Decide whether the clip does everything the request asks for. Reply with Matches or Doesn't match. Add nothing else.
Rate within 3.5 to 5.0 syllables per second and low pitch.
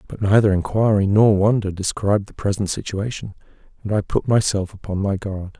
Doesn't match